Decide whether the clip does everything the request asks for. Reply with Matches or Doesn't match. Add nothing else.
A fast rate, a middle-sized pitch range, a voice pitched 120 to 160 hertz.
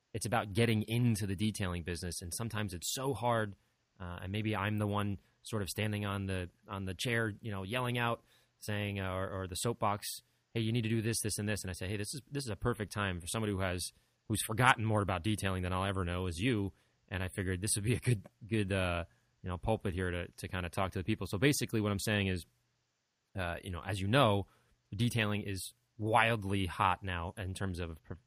Doesn't match